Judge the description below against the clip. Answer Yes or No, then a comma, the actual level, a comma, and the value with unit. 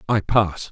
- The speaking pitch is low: Yes, very low, 95 Hz